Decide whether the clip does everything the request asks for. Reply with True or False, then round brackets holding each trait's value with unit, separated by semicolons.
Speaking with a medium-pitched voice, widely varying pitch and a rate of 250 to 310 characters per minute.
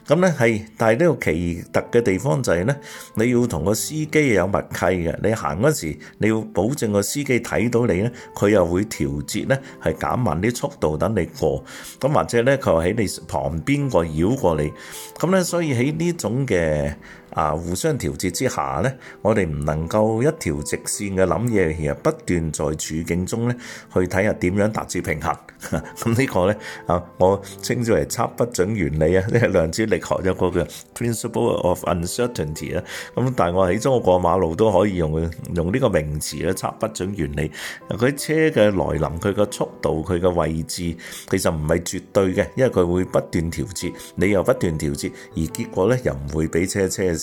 False (95 Hz; 6.0 semitones; 300 characters per minute)